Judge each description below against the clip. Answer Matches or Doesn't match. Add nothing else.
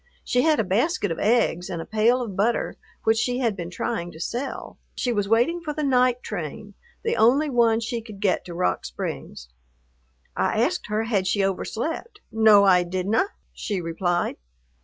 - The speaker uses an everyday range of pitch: Matches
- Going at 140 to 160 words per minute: Doesn't match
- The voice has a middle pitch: Doesn't match